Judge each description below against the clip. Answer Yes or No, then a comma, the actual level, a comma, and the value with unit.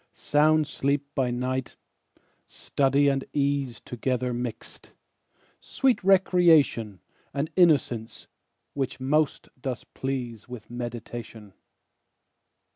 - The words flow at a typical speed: No, slow, 90 wpm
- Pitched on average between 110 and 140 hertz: Yes, low, 135 Hz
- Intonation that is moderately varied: Yes, average, 3.1 semitones